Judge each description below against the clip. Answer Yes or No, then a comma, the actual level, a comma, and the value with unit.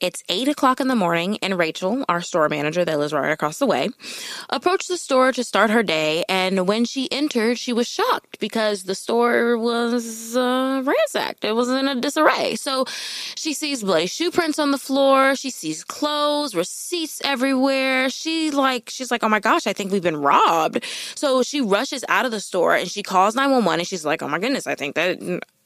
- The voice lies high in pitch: Yes, high, 245 Hz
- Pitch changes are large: Yes, wide, 6.2 semitones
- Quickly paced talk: Yes, fast, 210 wpm